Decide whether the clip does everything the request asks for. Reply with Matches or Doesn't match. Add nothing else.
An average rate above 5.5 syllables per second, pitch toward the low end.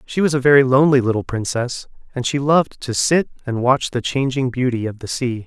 Matches